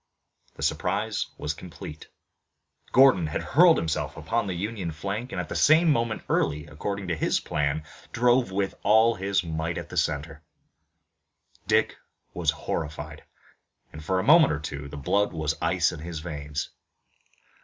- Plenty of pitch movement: Yes, wide, 6.0 semitones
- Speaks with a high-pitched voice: No, very low, 90 Hz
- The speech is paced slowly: No, average, 155 wpm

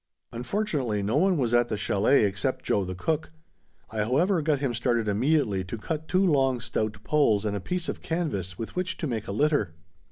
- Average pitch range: No, wide, 6.7 semitones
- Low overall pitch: Yes, low, 120 Hz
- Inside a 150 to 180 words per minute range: No, average, 200 wpm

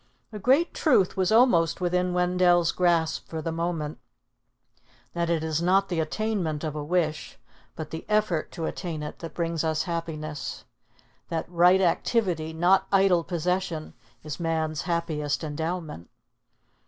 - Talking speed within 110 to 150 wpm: Yes, average, 140 wpm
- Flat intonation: Yes, narrow, 2.3 semitones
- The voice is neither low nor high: Yes, medium, 170 Hz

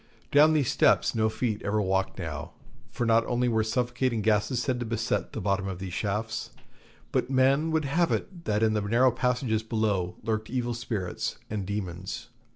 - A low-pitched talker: Yes, low, 110 Hz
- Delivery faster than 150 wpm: Yes, average, 180 wpm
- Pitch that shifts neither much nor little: Yes, average, 3.1 semitones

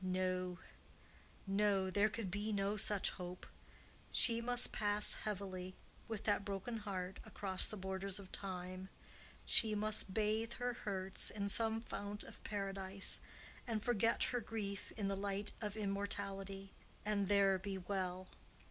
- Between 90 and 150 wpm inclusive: Yes, average, 140 wpm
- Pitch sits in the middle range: No, high, 200 Hz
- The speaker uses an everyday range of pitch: No, narrow, 1.9 semitones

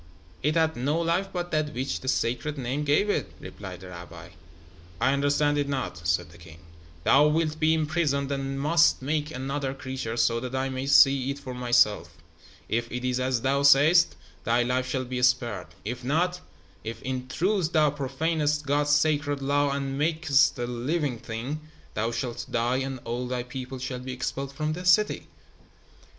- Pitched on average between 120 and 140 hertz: Yes, low, 135 Hz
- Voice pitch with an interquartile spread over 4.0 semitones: No, average, 3.2 semitones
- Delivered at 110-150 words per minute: No, average, 180 wpm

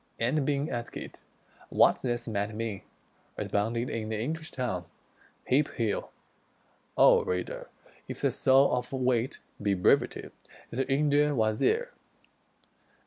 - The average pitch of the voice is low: Yes, low, 120 Hz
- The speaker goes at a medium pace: No, slow, 130 wpm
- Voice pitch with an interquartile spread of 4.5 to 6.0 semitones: No, average, 4.1 semitones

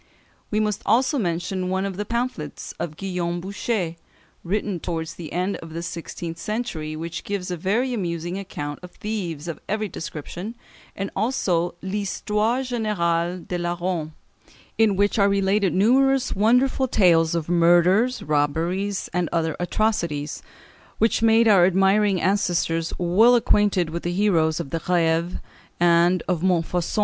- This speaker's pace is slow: No, average, 145 wpm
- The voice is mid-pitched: Yes, medium, 180 Hz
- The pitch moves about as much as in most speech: Yes, average, 3.7 semitones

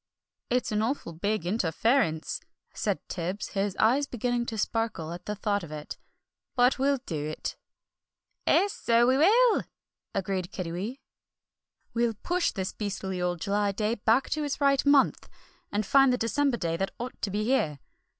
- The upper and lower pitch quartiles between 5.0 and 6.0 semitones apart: Yes, wide, 5.4 semitones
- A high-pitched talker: Yes, high, 215 Hz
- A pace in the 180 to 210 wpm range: No, average, 160 wpm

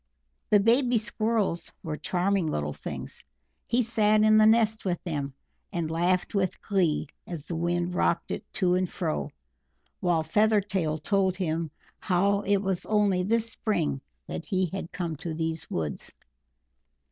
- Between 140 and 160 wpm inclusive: Yes, average, 150 wpm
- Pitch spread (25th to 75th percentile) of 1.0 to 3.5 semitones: No, average, 4.1 semitones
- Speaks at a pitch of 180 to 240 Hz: Yes, medium, 185 Hz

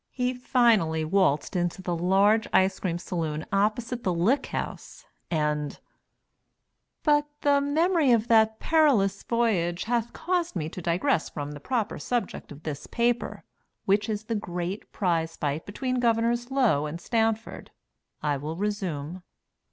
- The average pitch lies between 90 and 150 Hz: No, high, 205 Hz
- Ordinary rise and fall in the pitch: No, wide, 6.0 semitones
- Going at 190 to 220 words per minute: No, average, 145 wpm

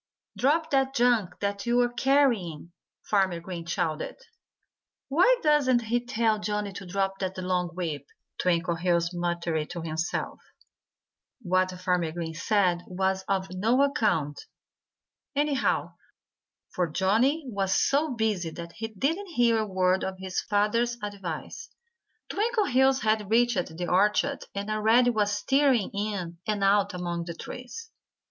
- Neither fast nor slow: No, slow, 130 wpm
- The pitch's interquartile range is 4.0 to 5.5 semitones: Yes, average, 5.2 semitones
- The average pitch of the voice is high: Yes, high, 200 Hz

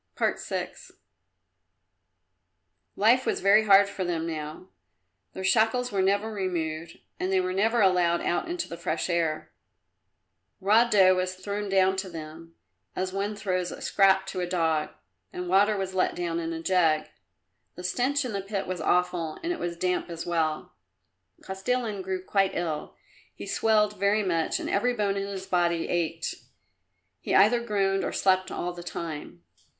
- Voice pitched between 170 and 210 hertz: Yes, medium, 185 Hz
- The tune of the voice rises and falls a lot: No, average, 2.8 semitones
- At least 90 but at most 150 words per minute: No, average, 165 wpm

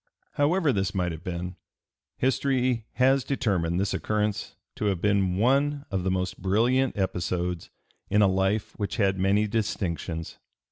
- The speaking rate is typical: Yes, average, 145 wpm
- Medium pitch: No, low, 100 Hz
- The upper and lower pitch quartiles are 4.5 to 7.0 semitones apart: Yes, average, 5.1 semitones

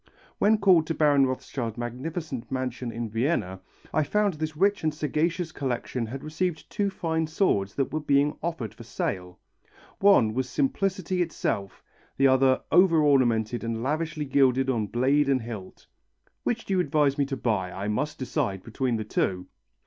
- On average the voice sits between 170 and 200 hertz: No, low, 135 Hz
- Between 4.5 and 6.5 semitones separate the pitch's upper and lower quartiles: Yes, wide, 5.4 semitones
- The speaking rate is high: No, average, 165 wpm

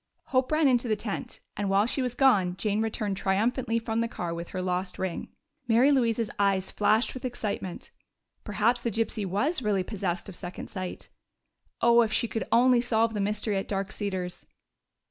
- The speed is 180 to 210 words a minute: Yes, average, 185 wpm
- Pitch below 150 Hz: No, high, 215 Hz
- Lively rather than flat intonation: No, average, 3.5 semitones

